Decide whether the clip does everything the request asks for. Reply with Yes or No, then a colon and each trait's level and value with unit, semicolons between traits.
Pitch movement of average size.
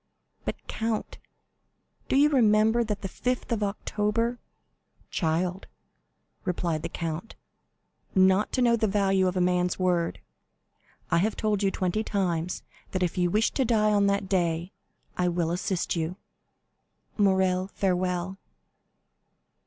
Yes: average, 3.0 semitones